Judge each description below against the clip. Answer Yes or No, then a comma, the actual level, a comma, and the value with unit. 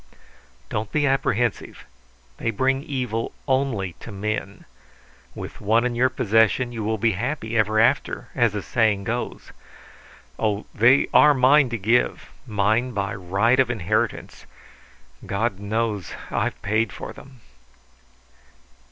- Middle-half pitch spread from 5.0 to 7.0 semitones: No, average, 3.2 semitones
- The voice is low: Yes, low, 115 Hz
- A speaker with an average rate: No, slow, 130 wpm